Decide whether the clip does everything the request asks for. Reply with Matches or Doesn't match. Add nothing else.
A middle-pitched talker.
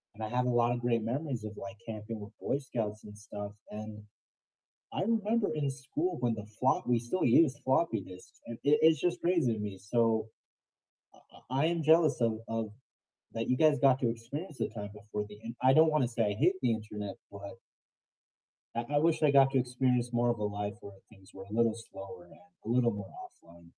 Doesn't match